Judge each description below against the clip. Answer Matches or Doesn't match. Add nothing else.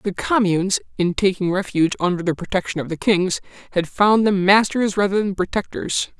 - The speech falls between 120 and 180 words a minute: Matches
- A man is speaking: Matches